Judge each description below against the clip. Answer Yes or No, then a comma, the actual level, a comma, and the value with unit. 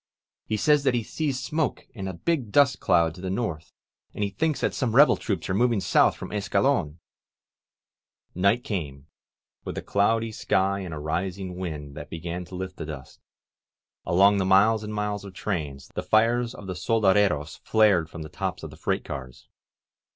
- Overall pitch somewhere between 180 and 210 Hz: No, low, 100 Hz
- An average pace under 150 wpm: No, average, 185 wpm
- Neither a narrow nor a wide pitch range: Yes, average, 4.7 semitones